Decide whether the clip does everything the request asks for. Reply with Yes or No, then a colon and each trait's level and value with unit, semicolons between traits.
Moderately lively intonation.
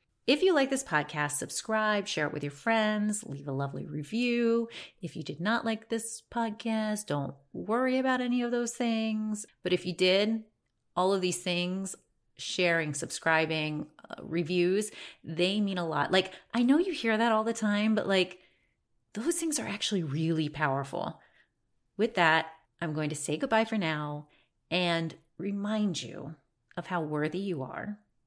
No: wide, 5.8 semitones